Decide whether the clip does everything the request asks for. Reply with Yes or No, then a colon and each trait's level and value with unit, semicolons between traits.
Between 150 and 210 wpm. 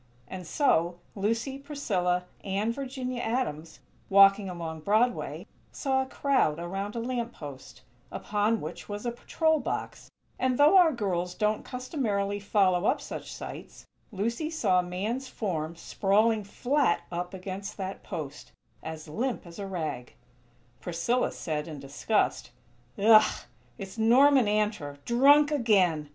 No: slow, 135 wpm